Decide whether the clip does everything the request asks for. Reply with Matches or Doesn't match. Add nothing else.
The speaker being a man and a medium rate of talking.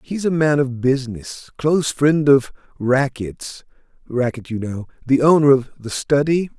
Matches